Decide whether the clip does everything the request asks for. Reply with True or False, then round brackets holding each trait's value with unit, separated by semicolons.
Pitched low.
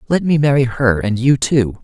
True (130 Hz)